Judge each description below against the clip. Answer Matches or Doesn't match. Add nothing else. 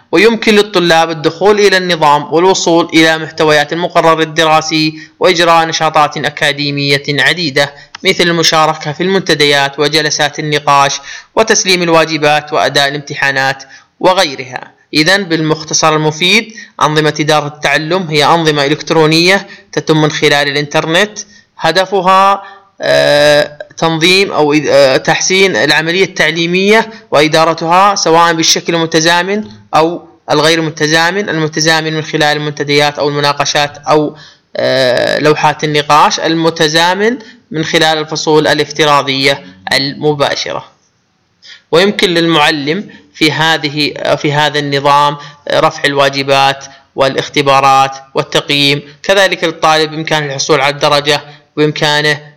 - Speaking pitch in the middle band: Matches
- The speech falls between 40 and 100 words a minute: Matches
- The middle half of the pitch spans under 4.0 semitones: Matches